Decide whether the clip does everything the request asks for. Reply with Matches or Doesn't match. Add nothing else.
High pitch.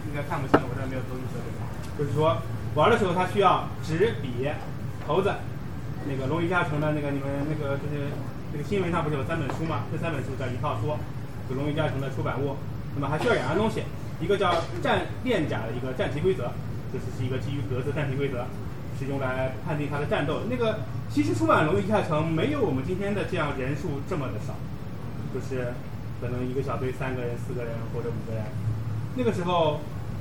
Doesn't match